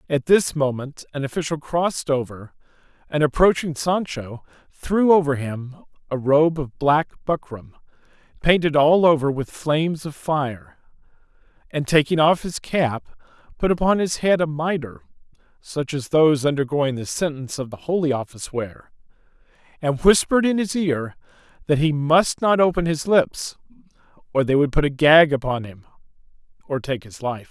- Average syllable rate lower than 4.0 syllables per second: No, 4.8 syllables/s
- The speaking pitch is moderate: Yes, medium, 150 Hz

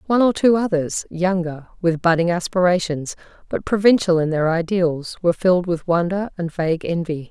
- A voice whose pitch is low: No, medium, 175 Hz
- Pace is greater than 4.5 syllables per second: Yes, 5.4 syllables/s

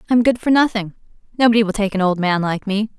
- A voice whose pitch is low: No, high, 210 Hz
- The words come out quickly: Yes, fast, 260 wpm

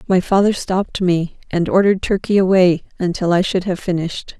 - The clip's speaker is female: Yes, female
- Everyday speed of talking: Yes, average, 180 wpm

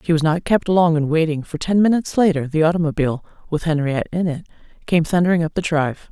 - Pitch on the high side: No, medium, 165 Hz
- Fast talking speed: Yes, fast, 215 wpm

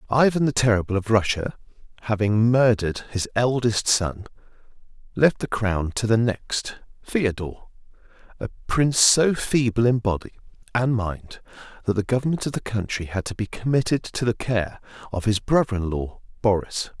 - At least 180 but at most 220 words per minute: No, average, 155 wpm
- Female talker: No, male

